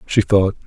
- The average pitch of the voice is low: Yes, low, 100 Hz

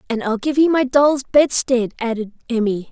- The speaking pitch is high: Yes, very high, 250 Hz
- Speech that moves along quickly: No, average, 185 wpm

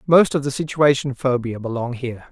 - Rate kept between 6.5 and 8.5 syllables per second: No, 5.5 syllables/s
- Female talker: No, male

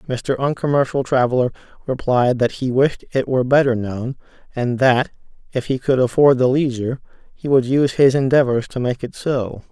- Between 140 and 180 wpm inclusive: Yes, average, 175 wpm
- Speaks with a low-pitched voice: Yes, low, 130 Hz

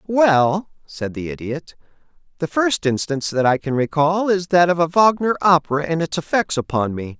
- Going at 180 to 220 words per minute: Yes, average, 185 wpm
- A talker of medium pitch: Yes, medium, 160 Hz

